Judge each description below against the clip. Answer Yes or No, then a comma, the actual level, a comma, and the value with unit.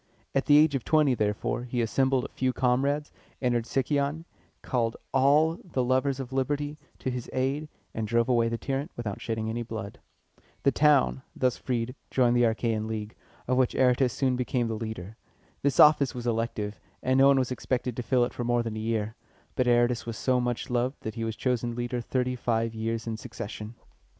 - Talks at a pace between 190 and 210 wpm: Yes, average, 195 wpm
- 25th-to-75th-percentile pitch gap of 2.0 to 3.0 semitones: Yes, narrow, 2.6 semitones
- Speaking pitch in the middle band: No, low, 125 Hz